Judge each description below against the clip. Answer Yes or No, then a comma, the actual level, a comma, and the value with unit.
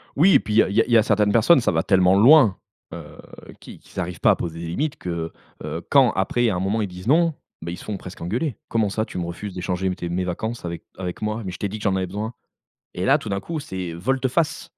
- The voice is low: Yes, low, 100 Hz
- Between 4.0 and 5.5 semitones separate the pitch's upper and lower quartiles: Yes, average, 4.5 semitones